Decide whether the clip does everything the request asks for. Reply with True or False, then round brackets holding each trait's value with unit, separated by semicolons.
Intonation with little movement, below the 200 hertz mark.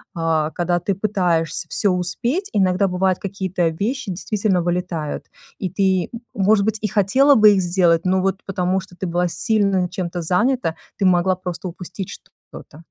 True (2.2 semitones; 185 Hz)